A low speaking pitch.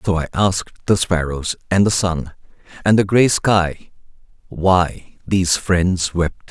Yes: very low, 90 Hz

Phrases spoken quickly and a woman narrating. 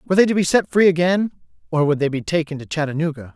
No: fast, 250 wpm; male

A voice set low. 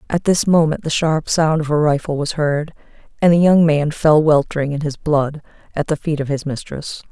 No: medium, 155 Hz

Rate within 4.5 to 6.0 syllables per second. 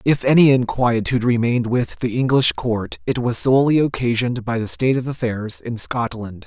Yes: 5.4 syllables/s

